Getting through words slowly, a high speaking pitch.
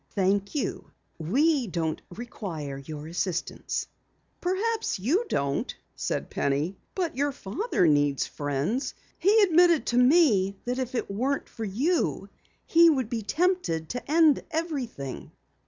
Yes: slow, 125 wpm; high, 245 Hz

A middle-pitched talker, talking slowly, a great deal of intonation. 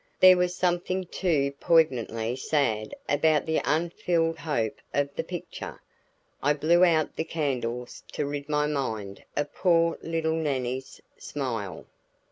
No: medium, 150 Hz; slow, 130 wpm; average, 4.0 semitones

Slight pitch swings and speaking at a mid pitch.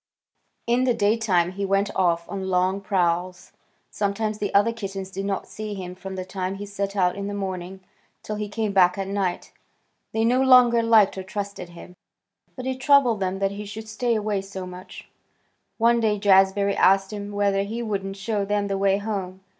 No: narrow, 2.0 semitones; high, 200 Hz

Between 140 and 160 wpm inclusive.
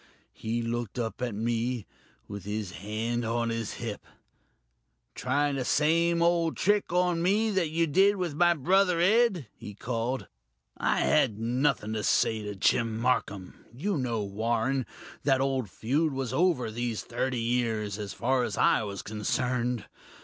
Yes: average, 155 wpm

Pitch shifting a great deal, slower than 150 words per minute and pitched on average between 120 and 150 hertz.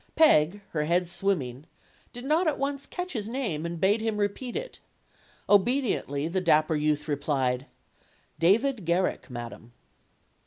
No: wide, 8.2 semitones; average, 140 wpm; medium, 185 Hz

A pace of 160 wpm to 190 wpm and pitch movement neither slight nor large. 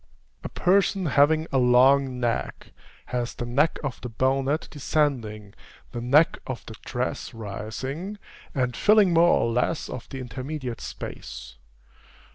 No: slow, 135 wpm; average, 4.0 semitones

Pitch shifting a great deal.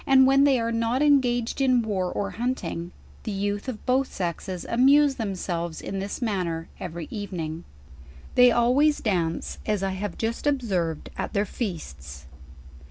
Yes: wide, 5.9 semitones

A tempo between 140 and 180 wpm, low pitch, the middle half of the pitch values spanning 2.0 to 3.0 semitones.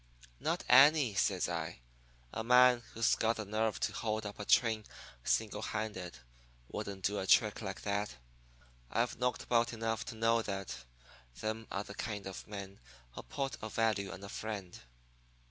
Yes: average, 165 wpm; low, 110 Hz; narrow, 2.4 semitones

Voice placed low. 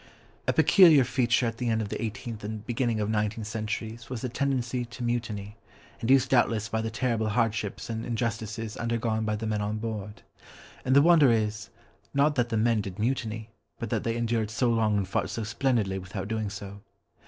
Yes: low, 115 Hz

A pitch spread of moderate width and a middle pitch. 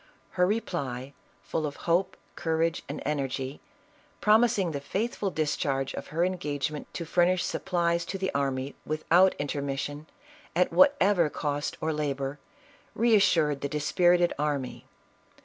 Yes: average, 4.1 semitones; medium, 155 Hz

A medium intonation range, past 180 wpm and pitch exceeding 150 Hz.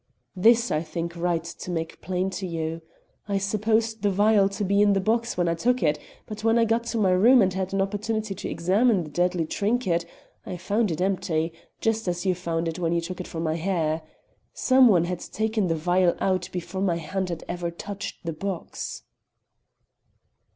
Yes: average, 3.8 semitones; fast, 205 wpm; medium, 185 Hz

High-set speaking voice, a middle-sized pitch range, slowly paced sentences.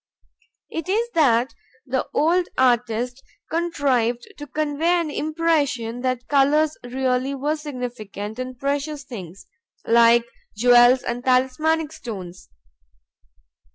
Yes: very high, 260 Hz; average, 3.9 semitones; slow, 105 wpm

